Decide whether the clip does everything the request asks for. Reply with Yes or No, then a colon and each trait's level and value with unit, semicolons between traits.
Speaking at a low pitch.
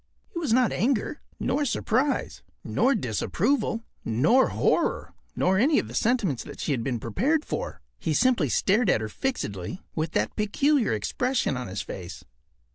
No: high, 210 Hz